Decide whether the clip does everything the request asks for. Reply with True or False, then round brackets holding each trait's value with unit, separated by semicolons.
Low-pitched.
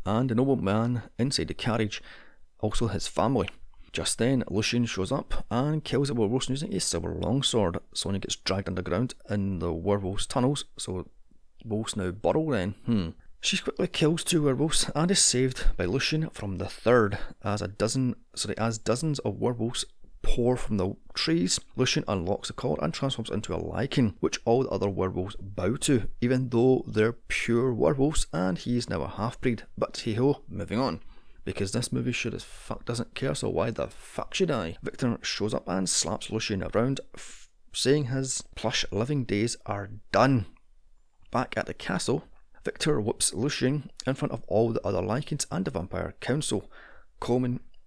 True (115 Hz)